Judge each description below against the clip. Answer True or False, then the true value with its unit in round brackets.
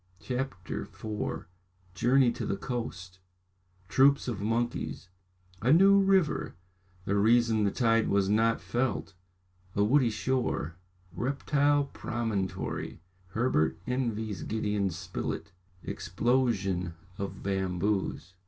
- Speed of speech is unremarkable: False (100 wpm)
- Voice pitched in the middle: False (110 Hz)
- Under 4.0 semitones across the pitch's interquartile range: False (4.7 semitones)